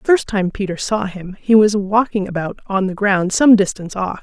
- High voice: Yes, high, 200 Hz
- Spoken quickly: Yes, fast, 225 wpm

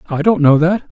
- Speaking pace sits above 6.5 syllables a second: No, 4.9 syllables/s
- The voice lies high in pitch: No, medium, 165 Hz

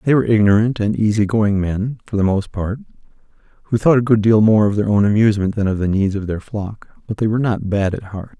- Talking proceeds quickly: Yes, fast, 245 wpm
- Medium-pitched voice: No, low, 105 Hz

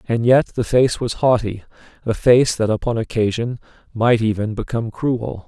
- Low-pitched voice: Yes, low, 115 Hz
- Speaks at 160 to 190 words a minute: Yes, average, 165 wpm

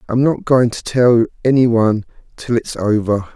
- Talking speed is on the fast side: No, average, 180 wpm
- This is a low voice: Yes, low, 115 Hz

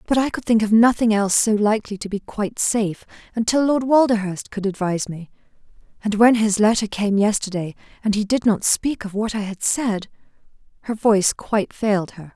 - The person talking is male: No, female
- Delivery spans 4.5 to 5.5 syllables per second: No, 5.7 syllables/s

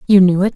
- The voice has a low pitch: No, high, 190 Hz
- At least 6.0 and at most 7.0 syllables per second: No, 7.7 syllables/s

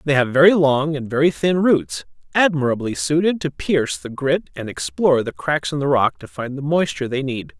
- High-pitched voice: No, medium, 140 Hz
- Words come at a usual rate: No, fast, 215 wpm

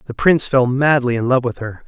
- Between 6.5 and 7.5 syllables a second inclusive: No, 5.9 syllables/s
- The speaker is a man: Yes, male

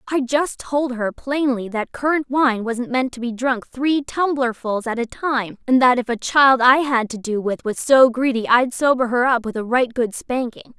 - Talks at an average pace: No, fast, 220 wpm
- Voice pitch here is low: No, very high, 250 Hz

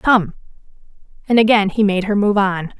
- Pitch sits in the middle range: No, high, 205 Hz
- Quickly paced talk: No, average, 170 wpm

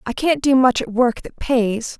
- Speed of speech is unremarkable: No, fast, 240 wpm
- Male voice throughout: No, female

